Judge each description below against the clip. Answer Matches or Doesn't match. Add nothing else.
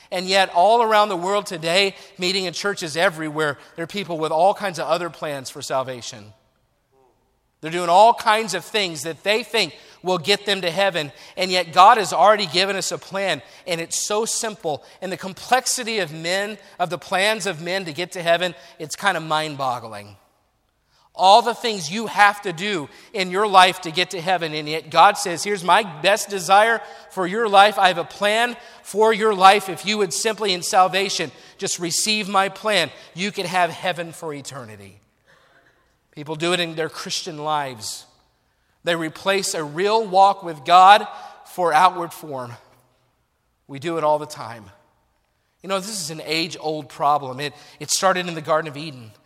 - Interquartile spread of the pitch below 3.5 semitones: Doesn't match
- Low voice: Doesn't match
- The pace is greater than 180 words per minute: Matches